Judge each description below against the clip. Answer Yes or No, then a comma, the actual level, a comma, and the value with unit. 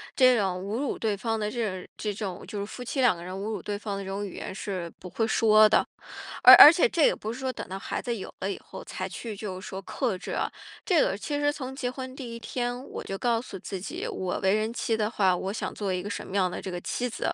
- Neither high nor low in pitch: No, high, 215 Hz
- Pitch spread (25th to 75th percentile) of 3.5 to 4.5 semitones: Yes, average, 4.1 semitones